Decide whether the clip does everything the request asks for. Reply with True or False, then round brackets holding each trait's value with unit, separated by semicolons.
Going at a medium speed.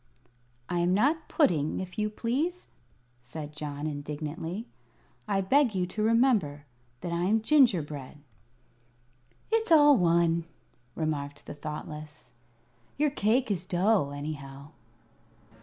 False (115 wpm)